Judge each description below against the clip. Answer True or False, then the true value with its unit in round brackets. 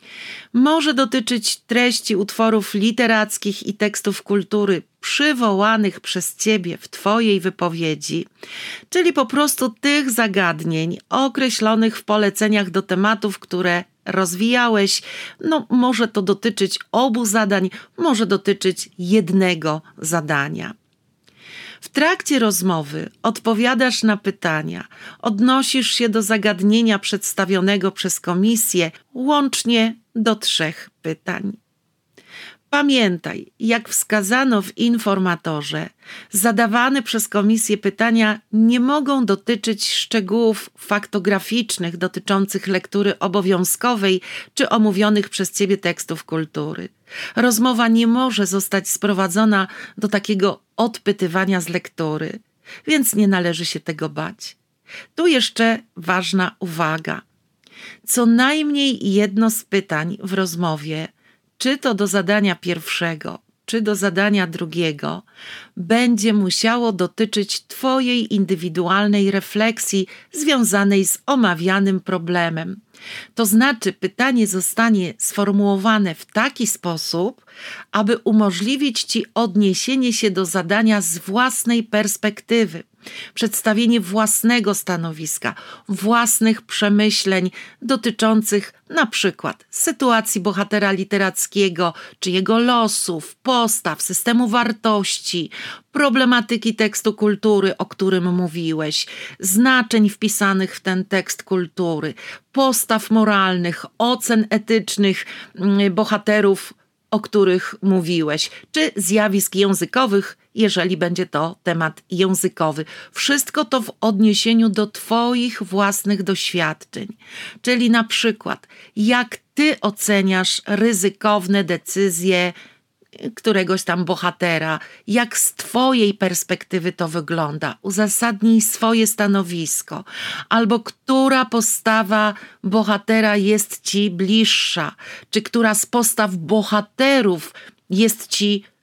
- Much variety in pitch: False (3.3 semitones)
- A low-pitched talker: False (210 Hz)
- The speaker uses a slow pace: True (100 wpm)